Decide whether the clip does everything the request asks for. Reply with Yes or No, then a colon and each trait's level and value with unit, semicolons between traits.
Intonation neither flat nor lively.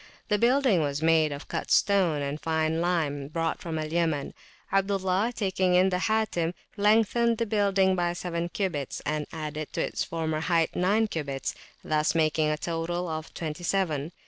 Yes: average, 3.7 semitones